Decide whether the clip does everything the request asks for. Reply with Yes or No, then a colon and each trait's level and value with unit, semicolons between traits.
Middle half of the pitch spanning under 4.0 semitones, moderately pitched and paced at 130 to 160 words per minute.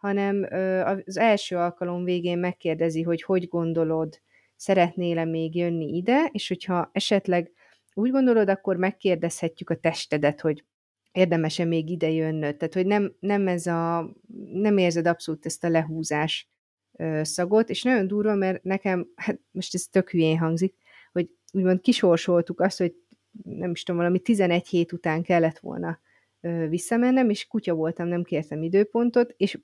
Yes: average, 2.9 semitones; medium, 180 Hz; average, 150 wpm